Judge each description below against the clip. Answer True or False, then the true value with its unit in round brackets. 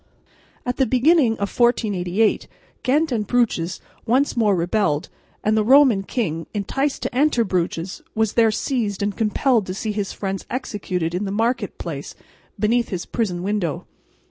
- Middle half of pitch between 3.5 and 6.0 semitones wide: True (4.4 semitones)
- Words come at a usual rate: True (155 wpm)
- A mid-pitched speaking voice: False (215 Hz)